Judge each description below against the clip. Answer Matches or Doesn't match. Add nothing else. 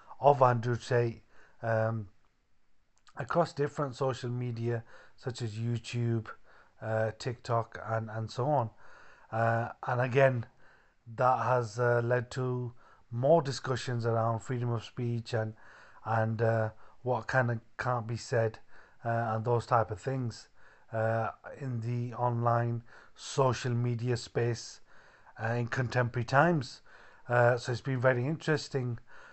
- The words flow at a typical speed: Doesn't match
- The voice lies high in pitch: Doesn't match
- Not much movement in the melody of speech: Matches